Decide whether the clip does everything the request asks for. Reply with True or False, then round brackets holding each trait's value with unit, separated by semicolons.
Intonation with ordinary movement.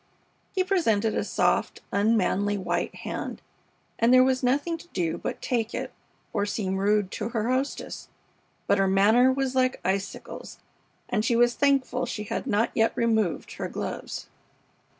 True (4.0 semitones)